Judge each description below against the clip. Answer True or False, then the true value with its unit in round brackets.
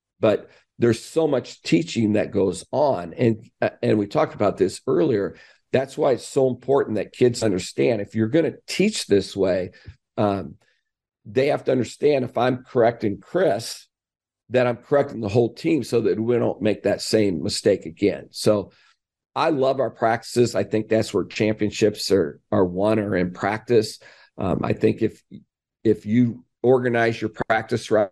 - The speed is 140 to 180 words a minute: True (170 wpm)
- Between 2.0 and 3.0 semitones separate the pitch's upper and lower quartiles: True (2.6 semitones)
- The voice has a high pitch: False (115 Hz)